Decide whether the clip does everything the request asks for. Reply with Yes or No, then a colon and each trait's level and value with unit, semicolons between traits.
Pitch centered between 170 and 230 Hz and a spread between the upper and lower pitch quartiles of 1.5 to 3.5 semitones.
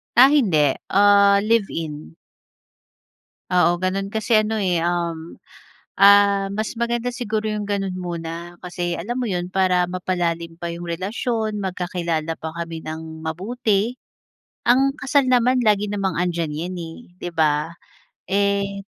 No: medium, 185 Hz; average, 3.9 semitones